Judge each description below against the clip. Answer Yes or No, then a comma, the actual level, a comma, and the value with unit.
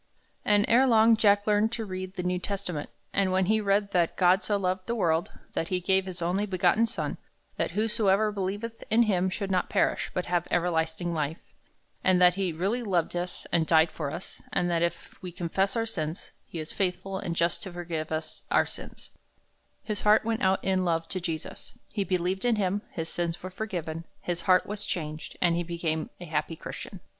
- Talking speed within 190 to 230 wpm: Yes, average, 200 wpm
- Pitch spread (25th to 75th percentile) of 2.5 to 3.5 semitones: Yes, average, 3.0 semitones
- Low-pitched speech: No, medium, 185 Hz